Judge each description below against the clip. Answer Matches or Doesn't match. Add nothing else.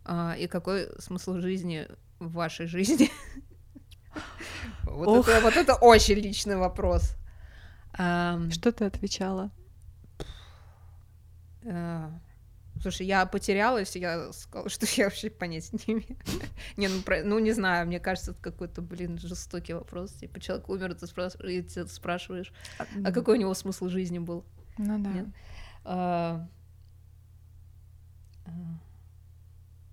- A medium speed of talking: Doesn't match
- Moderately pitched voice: Matches